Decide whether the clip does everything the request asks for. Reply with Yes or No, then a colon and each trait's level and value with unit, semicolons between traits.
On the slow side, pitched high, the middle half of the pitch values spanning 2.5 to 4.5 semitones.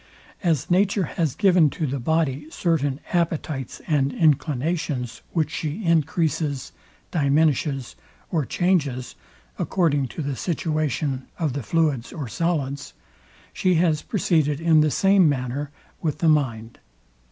No: slow, 125 wpm; medium, 155 Hz; average, 3.3 semitones